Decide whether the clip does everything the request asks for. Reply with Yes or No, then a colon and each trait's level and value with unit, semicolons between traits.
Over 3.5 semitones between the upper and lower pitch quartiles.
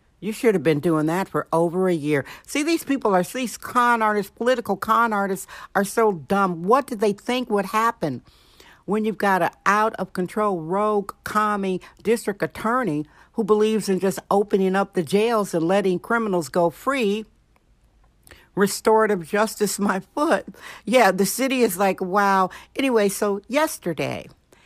No: average, 3.0 semitones